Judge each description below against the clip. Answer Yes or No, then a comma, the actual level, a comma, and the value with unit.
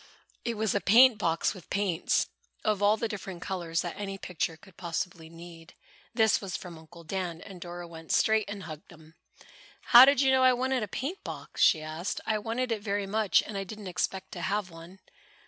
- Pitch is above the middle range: Yes, high, 195 Hz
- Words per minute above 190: Yes, fast, 205 wpm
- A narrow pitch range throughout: No, average, 4.1 semitones